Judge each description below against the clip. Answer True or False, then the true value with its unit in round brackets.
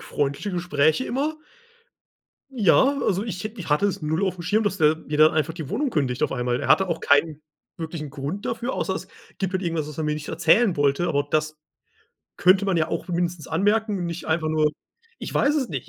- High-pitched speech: False (165 Hz)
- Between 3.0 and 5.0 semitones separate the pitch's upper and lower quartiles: True (4.5 semitones)